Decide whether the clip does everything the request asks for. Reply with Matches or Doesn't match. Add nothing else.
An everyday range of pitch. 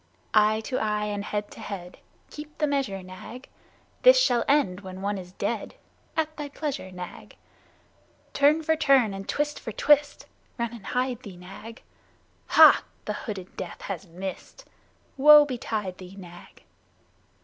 Doesn't match